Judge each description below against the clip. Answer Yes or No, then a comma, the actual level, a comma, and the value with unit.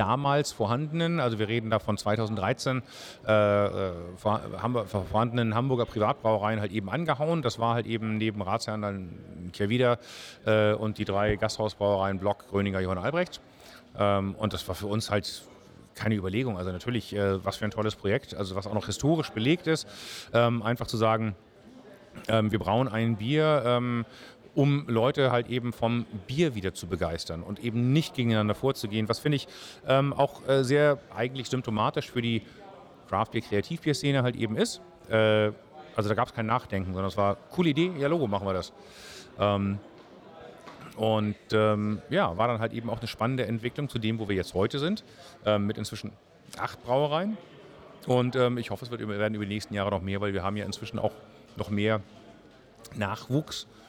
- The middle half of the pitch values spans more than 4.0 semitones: No, average, 3.2 semitones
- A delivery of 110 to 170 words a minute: No, average, 185 wpm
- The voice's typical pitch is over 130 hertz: No, low, 110 Hz